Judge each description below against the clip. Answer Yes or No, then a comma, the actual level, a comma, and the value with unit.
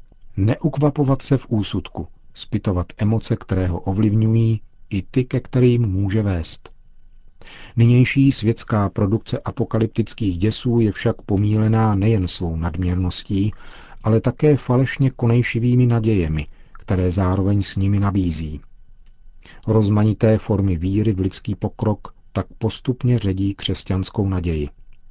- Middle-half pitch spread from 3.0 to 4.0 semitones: Yes, average, 3.3 semitones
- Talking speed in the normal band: No, slow, 110 wpm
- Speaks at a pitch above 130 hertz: No, low, 105 Hz